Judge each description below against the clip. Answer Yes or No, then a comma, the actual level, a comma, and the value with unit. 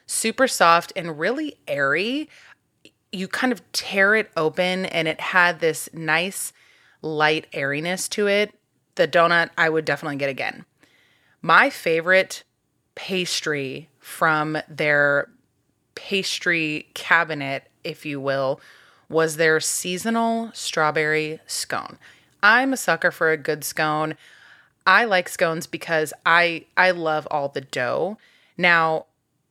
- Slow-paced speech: Yes, slow, 120 wpm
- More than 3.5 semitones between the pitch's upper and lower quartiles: No, average, 3.2 semitones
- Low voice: No, medium, 165 Hz